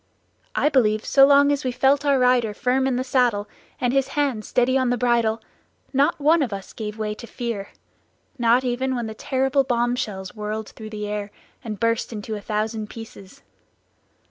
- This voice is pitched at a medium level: No, high, 240 Hz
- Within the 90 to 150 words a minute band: No, average, 190 wpm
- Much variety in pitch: No, average, 3.5 semitones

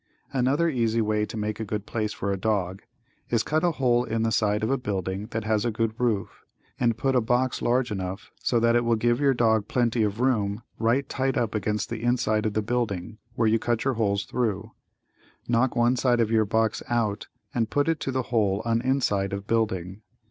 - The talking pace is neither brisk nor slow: No, fast, 220 wpm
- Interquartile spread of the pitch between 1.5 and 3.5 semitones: Yes, narrow, 2.5 semitones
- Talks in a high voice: No, low, 115 Hz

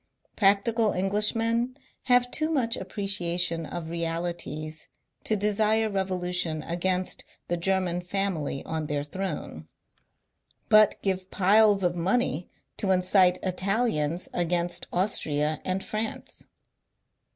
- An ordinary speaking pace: No, slow, 105 wpm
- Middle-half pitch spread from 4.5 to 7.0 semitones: No, average, 3.5 semitones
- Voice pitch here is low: No, medium, 185 Hz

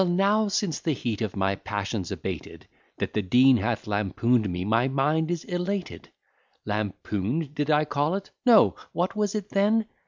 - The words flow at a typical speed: Yes, average, 165 wpm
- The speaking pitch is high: No, medium, 145 Hz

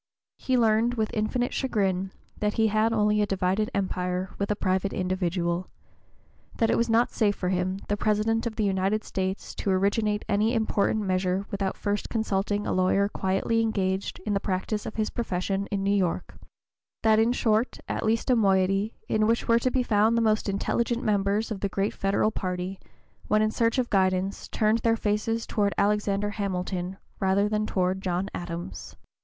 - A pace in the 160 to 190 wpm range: Yes, average, 185 wpm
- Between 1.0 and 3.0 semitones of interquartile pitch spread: Yes, narrow, 2.5 semitones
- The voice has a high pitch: Yes, high, 205 Hz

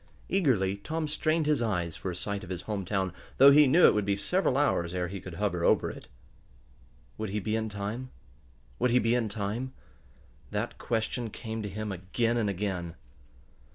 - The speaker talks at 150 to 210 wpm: Yes, average, 190 wpm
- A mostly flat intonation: No, average, 4.3 semitones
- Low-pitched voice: Yes, low, 105 Hz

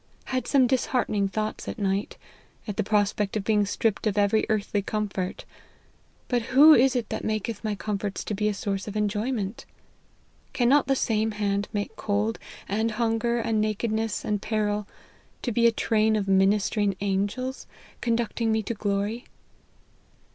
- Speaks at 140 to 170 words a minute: Yes, average, 160 wpm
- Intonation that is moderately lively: No, narrow, 2.1 semitones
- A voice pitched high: Yes, high, 215 Hz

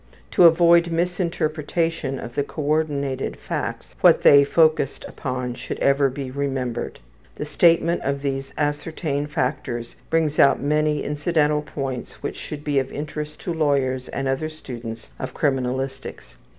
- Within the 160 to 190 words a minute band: No, average, 140 wpm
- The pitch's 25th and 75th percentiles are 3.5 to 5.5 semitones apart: No, average, 2.7 semitones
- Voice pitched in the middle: Yes, medium, 145 Hz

